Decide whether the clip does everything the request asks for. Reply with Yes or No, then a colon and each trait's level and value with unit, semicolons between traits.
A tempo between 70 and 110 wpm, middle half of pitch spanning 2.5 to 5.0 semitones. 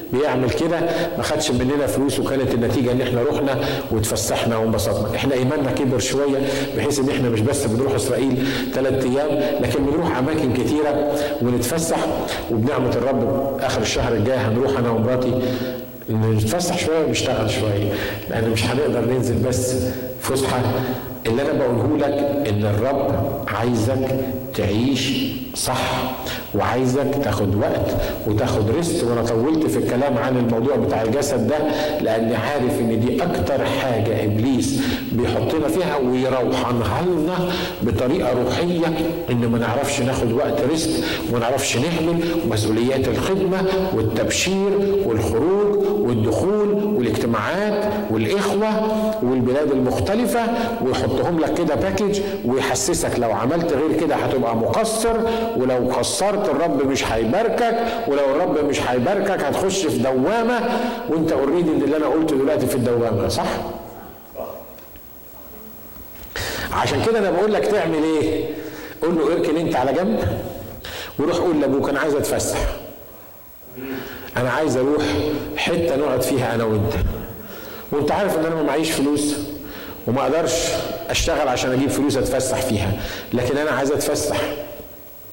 No: average, 125 wpm; average, 4.5 semitones